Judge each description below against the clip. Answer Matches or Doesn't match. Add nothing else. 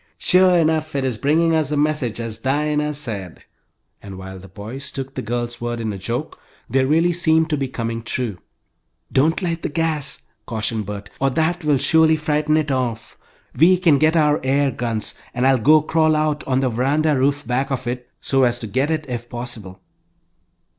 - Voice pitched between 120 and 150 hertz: Matches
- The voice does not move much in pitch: Doesn't match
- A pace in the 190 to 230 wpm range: Matches